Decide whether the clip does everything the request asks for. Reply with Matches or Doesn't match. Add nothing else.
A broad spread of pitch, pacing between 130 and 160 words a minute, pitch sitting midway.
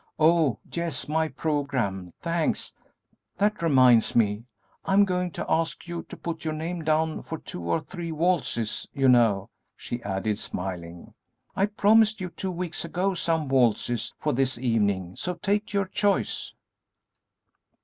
Matches